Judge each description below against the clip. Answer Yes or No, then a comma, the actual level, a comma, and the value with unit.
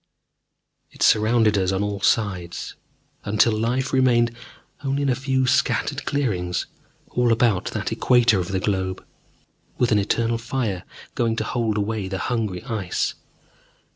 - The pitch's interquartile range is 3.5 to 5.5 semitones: Yes, average, 3.8 semitones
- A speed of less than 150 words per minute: Yes, average, 140 wpm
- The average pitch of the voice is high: No, low, 110 Hz